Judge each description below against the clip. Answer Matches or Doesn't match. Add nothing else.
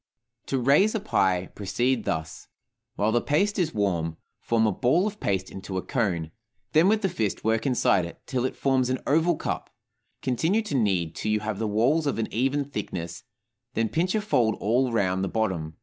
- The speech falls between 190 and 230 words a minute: Matches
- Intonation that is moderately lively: Doesn't match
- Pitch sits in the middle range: Doesn't match